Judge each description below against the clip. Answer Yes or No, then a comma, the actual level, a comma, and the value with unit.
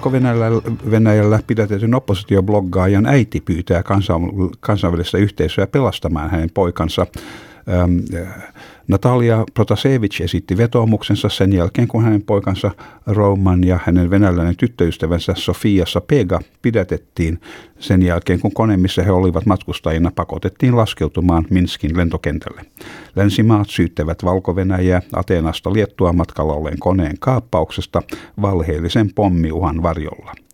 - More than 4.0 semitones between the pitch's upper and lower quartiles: No, average, 3.3 semitones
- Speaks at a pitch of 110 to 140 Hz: No, very low, 95 Hz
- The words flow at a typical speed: Yes, average, 105 wpm